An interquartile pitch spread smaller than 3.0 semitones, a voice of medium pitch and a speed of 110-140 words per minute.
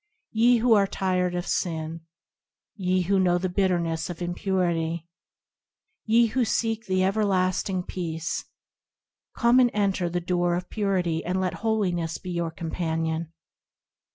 Yes: narrow, 2.5 semitones; medium, 180 Hz; slow, 135 wpm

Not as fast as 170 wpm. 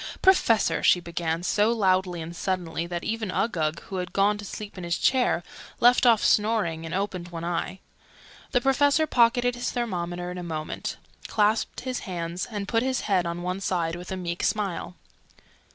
No: average, 180 wpm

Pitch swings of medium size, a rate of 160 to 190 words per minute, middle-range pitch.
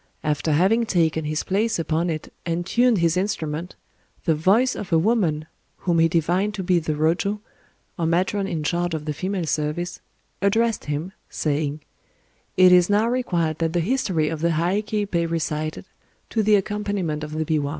Yes: average, 4.2 semitones; average, 170 wpm; medium, 170 Hz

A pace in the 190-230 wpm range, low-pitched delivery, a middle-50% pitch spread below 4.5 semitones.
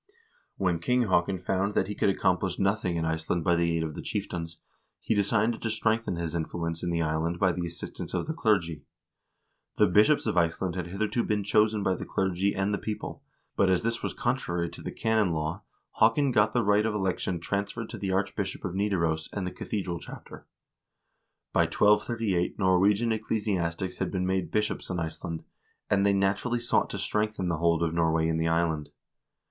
Yes: average, 195 wpm; very low, 95 Hz; average, 3.7 semitones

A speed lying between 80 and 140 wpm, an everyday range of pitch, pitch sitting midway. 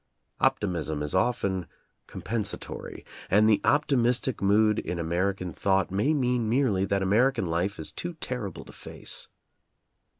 No: slow, 135 wpm; average, 4.7 semitones; low, 100 Hz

